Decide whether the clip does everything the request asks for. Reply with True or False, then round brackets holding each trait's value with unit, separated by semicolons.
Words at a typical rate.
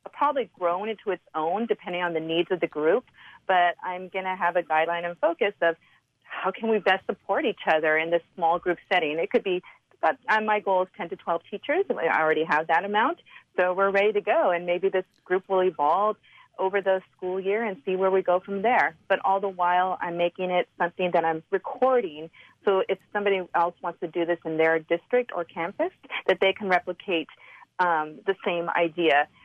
False (215 wpm)